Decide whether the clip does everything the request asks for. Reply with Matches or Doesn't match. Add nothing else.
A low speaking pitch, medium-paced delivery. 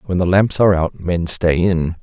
Doesn't match